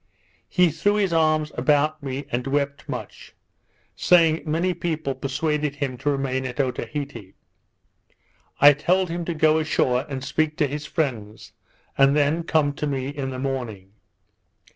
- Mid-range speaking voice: Yes, medium, 145 Hz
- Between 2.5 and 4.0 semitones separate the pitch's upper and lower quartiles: Yes, average, 2.8 semitones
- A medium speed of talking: Yes, average, 150 wpm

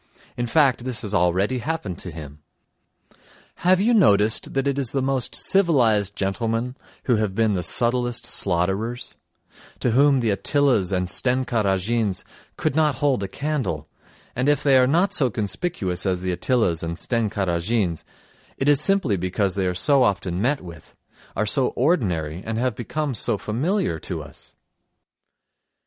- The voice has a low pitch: Yes, low, 115 Hz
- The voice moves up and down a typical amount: No, wide, 6.1 semitones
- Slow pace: No, average, 160 wpm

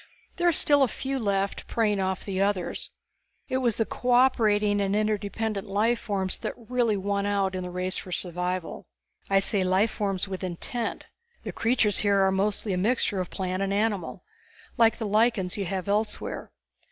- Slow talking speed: No, average, 175 wpm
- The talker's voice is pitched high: Yes, high, 205 Hz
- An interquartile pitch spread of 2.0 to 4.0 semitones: Yes, average, 2.8 semitones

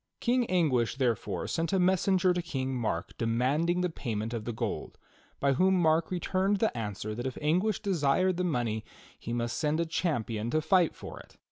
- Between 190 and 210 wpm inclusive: Yes, average, 195 wpm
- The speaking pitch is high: No, medium, 155 Hz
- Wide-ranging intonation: Yes, wide, 7.3 semitones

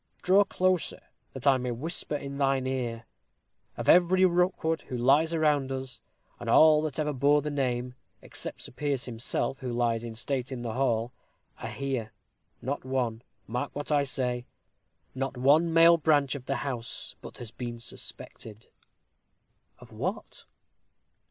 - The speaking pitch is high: No, low, 135 Hz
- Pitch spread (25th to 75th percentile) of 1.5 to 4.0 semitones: Yes, average, 3.5 semitones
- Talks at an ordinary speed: Yes, average, 160 wpm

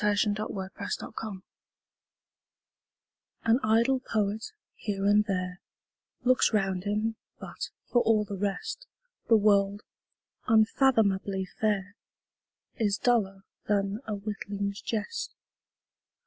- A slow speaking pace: Yes, slow, 105 wpm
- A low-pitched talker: No, high, 210 Hz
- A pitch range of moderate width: No, narrow, 2.0 semitones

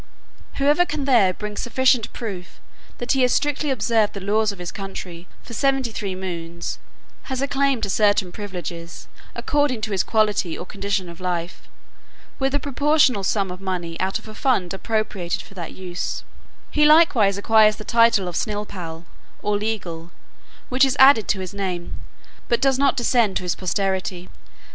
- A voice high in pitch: Yes, high, 205 Hz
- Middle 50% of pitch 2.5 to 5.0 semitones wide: No, wide, 5.4 semitones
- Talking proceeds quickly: No, average, 170 wpm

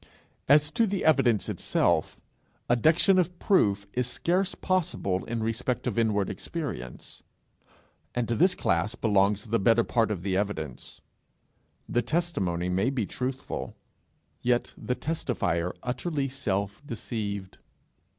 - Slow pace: Yes, slow, 125 wpm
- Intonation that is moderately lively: No, wide, 6.3 semitones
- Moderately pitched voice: No, low, 120 Hz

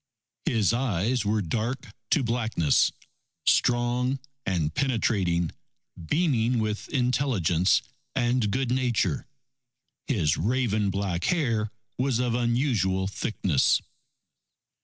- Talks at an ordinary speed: No, slow, 95 wpm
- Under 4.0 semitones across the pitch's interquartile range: No, average, 4.3 semitones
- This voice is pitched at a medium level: No, low, 115 Hz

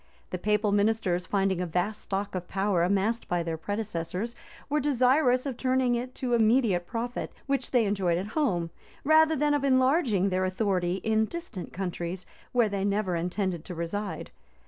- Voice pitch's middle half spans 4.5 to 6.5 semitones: Yes, average, 5.3 semitones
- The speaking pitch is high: Yes, high, 205 Hz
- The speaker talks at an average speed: Yes, average, 170 wpm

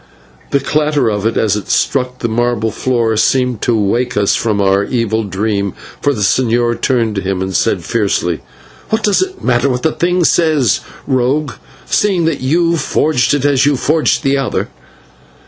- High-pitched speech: No, low, 125 Hz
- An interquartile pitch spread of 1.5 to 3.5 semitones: No, average, 4.7 semitones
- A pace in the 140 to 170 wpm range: No, average, 180 wpm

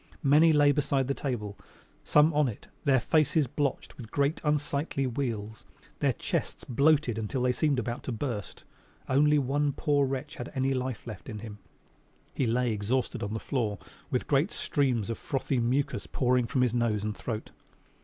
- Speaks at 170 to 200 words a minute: Yes, average, 175 wpm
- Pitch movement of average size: Yes, average, 3.8 semitones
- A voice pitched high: No, low, 130 Hz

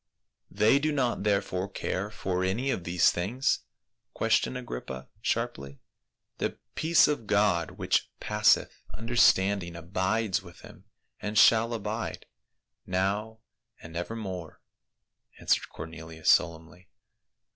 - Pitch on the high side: No, low, 100 Hz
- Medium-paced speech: No, slow, 115 wpm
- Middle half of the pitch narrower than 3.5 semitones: No, average, 4.5 semitones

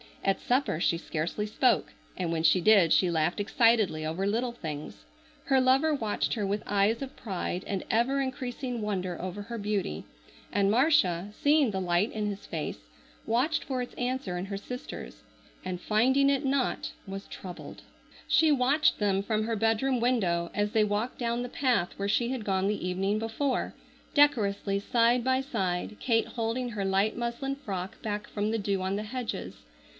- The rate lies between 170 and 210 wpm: Yes, average, 175 wpm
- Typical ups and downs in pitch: Yes, average, 4.5 semitones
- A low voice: No, high, 215 Hz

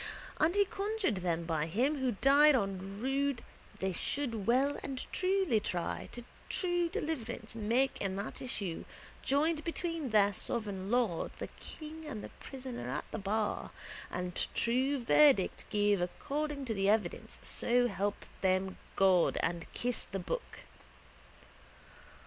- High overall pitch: Yes, high, 235 Hz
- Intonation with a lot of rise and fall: Yes, wide, 6.5 semitones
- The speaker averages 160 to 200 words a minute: No, average, 145 wpm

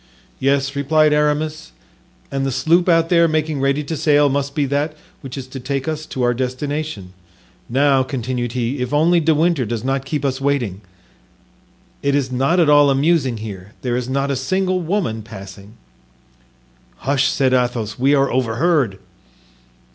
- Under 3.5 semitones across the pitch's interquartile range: Yes, average, 3.1 semitones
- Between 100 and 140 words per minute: No, average, 165 wpm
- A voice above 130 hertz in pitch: Yes, medium, 140 Hz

